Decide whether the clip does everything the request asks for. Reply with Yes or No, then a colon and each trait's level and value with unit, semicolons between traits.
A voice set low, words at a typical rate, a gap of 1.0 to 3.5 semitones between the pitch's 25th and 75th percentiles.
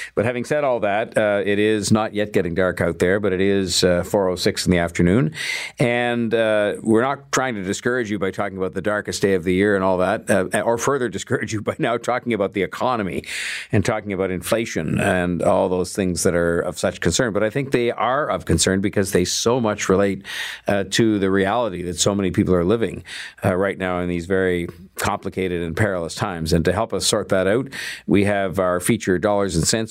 No: low, 100 Hz; fast, 225 wpm; average, 2.9 semitones